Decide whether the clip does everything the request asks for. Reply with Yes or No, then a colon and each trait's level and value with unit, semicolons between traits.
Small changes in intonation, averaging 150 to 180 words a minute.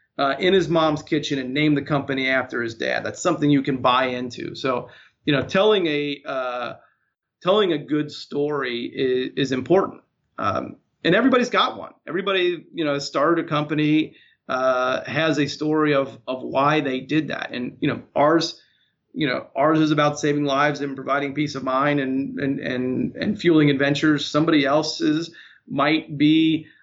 Yes: narrow, 2.3 semitones; average, 175 wpm